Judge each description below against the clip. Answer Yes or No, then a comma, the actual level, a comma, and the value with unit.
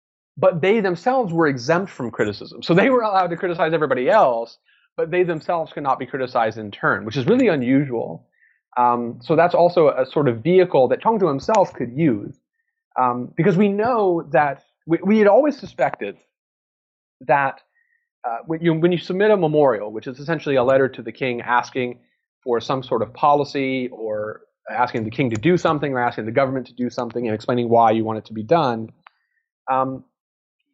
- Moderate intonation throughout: No, wide, 6.4 semitones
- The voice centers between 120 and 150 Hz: Yes, medium, 140 Hz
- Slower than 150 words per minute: No, average, 190 wpm